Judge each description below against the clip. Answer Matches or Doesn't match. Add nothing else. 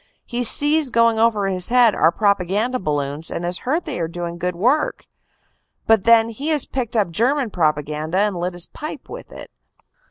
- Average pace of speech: Matches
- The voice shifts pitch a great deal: Matches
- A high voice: Matches